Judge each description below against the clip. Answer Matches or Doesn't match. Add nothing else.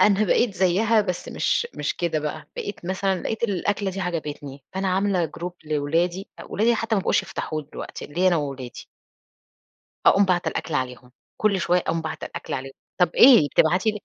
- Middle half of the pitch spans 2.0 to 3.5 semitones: Doesn't match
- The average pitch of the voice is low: Doesn't match